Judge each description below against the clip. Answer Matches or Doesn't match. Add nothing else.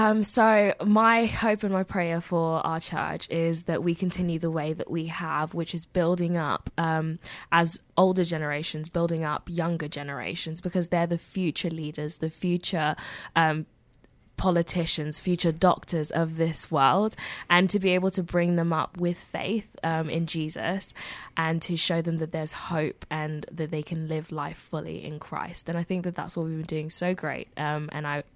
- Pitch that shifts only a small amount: Matches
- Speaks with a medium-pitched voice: Matches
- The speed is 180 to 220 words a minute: Matches